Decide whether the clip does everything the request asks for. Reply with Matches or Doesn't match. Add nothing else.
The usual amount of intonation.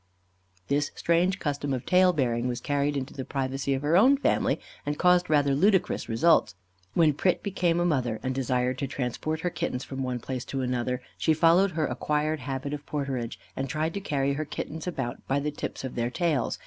Matches